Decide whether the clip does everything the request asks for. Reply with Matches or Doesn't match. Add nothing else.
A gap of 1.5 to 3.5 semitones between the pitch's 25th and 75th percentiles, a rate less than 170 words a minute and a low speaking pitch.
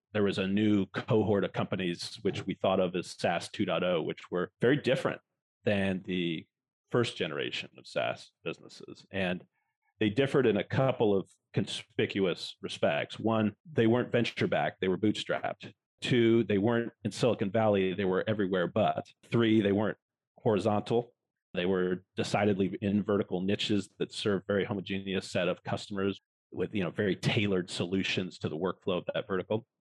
Matches